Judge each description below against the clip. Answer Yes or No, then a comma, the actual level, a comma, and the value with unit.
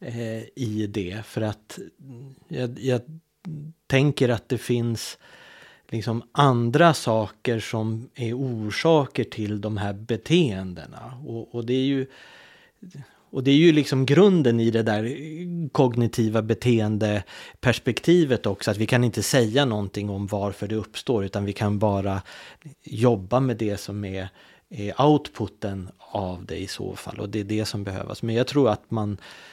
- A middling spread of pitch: Yes, average, 4.1 semitones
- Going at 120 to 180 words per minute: Yes, average, 150 wpm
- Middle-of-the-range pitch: No, low, 115 Hz